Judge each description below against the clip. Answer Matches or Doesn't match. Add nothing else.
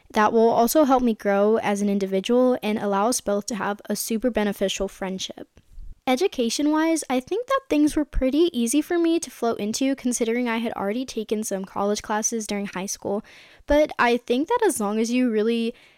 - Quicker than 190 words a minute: Matches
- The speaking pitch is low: Doesn't match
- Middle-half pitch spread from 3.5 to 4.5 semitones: Matches